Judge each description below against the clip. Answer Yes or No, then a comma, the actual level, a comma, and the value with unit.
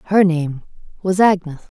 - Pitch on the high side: No, medium, 175 Hz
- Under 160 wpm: Yes, slow, 135 wpm